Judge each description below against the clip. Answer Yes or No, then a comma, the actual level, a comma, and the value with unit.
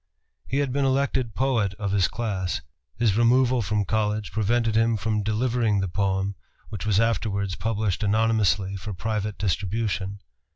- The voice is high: No, low, 110 Hz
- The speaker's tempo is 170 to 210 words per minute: No, average, 150 wpm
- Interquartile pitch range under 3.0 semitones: Yes, narrow, 2.5 semitones